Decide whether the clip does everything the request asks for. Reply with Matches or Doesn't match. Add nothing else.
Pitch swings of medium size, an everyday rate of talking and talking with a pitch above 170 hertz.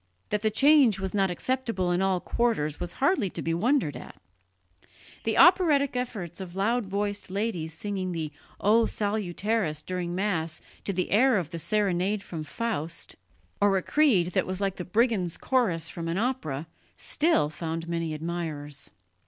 Matches